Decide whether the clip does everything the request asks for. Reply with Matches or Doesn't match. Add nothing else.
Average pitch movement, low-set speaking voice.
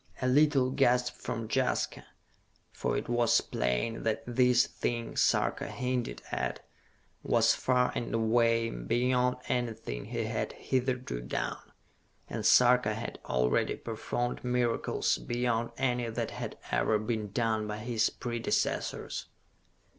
Doesn't match